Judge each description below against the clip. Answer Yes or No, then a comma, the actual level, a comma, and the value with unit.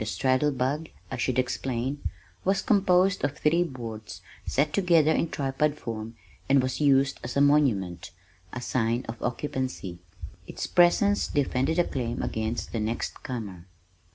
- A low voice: Yes, low, 130 Hz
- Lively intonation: No, average, 4.4 semitones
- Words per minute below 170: Yes, average, 150 wpm